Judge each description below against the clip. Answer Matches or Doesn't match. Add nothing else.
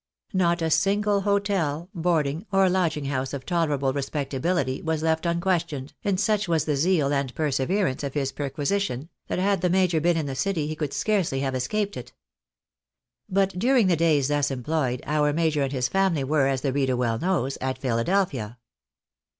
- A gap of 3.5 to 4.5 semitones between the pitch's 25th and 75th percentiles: Doesn't match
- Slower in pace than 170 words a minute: Doesn't match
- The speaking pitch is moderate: Matches